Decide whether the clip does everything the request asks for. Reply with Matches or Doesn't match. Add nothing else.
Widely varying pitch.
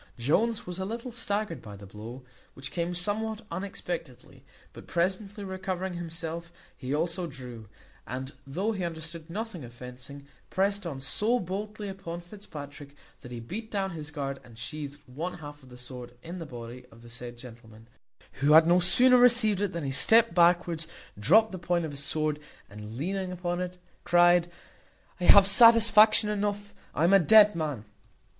Matches